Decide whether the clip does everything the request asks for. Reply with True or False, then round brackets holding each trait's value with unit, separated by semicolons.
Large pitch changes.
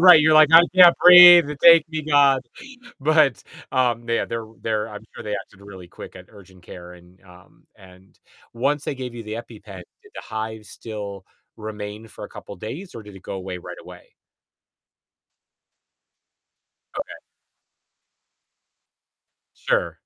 True (6.5 semitones)